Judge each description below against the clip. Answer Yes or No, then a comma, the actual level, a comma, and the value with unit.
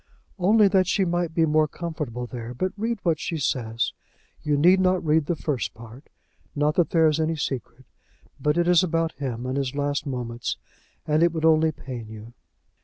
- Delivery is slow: No, average, 190 wpm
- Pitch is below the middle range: No, medium, 155 Hz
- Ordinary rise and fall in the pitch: Yes, average, 4.7 semitones